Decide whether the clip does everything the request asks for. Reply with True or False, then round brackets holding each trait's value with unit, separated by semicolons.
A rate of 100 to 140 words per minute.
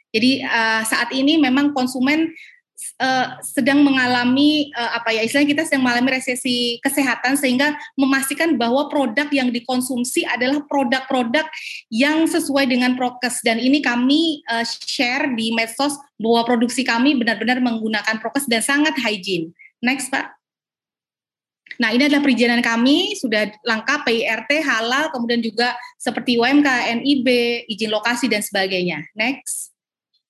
True (135 wpm)